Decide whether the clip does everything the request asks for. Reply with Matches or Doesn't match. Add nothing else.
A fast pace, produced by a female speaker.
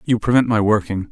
Doesn't match